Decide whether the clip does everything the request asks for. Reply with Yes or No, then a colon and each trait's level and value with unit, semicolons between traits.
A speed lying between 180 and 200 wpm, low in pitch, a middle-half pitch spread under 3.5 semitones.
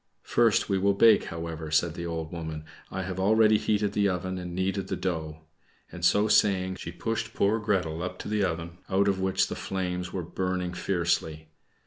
Yes: average, 190 wpm; very low, 95 Hz; average, 2.8 semitones